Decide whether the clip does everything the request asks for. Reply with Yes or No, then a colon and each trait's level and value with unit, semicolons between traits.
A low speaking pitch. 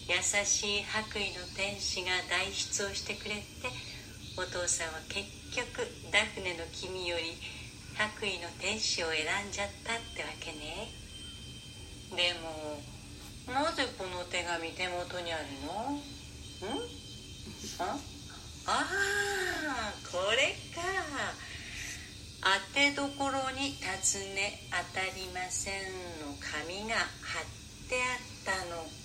No: medium, 185 Hz